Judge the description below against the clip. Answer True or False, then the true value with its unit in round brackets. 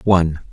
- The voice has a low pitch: True (85 Hz)